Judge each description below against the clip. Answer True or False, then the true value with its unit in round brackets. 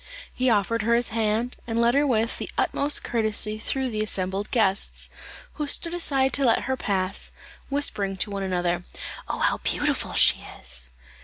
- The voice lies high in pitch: True (225 Hz)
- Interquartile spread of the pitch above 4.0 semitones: True (4.4 semitones)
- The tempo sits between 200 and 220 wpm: False (170 wpm)